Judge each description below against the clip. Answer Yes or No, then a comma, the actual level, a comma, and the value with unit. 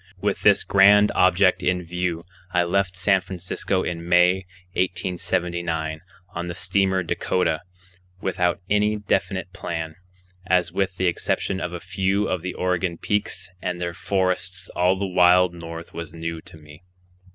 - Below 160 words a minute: Yes, average, 150 wpm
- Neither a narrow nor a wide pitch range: No, narrow, 1.6 semitones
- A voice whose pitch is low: Yes, very low, 90 Hz